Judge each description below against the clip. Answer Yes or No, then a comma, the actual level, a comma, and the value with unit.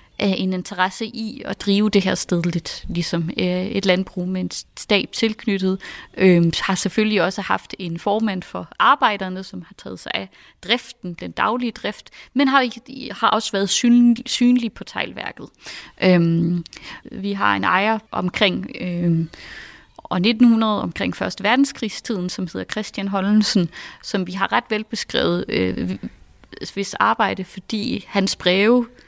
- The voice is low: No, high, 200 Hz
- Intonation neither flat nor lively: Yes, average, 3.5 semitones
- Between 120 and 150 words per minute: Yes, slow, 145 wpm